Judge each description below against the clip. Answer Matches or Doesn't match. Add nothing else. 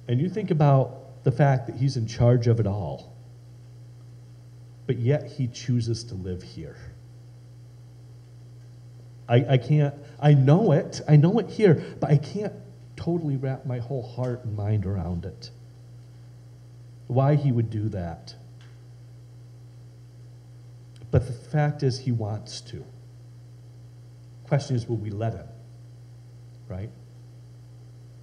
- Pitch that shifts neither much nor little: Doesn't match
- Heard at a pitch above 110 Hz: Matches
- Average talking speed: Doesn't match